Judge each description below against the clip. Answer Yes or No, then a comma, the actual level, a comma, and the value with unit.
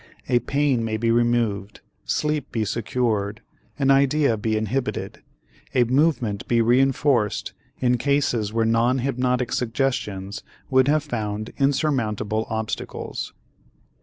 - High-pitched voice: No, low, 120 Hz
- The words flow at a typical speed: No, slow, 115 wpm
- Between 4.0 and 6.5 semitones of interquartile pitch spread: No, average, 3.6 semitones